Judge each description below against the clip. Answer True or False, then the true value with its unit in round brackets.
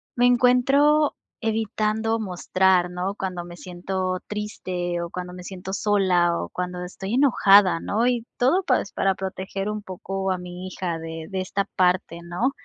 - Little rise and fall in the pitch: False (3.2 semitones)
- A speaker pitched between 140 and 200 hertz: True (190 Hz)